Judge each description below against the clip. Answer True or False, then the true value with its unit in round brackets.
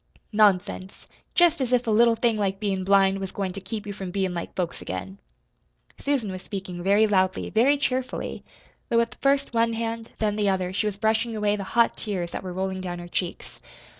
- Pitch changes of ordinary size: True (3.4 semitones)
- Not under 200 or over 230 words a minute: True (205 wpm)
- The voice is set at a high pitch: True (205 Hz)